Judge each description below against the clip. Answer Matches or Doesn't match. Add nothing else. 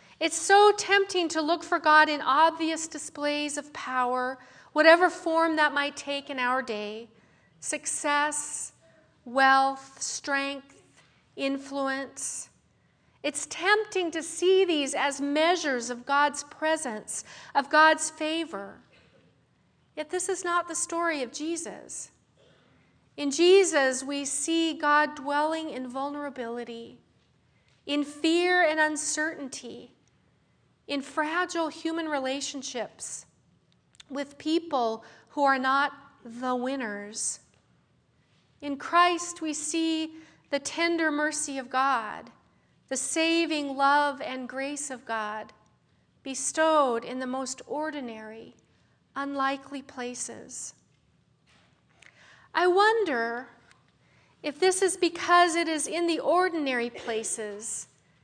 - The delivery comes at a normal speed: Doesn't match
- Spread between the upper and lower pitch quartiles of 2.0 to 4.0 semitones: Matches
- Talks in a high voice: Matches